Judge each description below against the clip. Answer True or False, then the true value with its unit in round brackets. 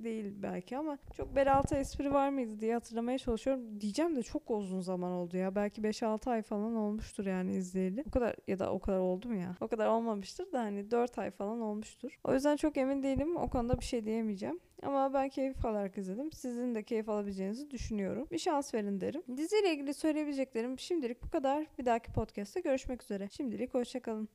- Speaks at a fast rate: True (195 wpm)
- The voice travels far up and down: False (4.6 semitones)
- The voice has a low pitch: False (235 Hz)